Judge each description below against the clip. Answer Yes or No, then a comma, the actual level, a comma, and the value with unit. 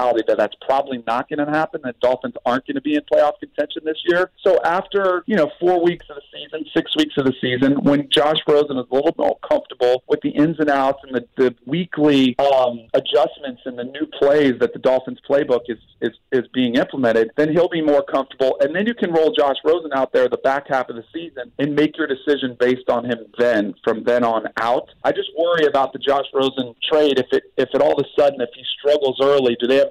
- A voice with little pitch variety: No, average, 3.4 semitones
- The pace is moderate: No, fast, 235 wpm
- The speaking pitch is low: No, medium, 145 Hz